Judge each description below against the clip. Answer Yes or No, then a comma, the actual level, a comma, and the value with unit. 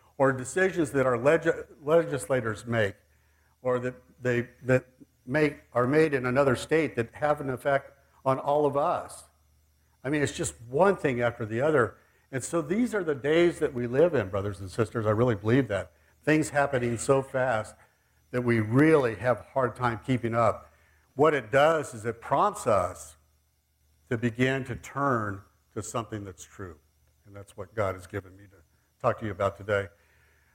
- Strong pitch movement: Yes, wide, 5.7 semitones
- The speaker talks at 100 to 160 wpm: No, average, 180 wpm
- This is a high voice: No, low, 120 Hz